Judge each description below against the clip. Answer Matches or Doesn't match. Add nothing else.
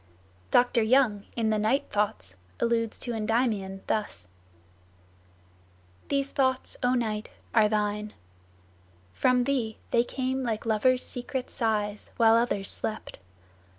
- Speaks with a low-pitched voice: Doesn't match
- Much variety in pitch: Doesn't match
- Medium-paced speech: Doesn't match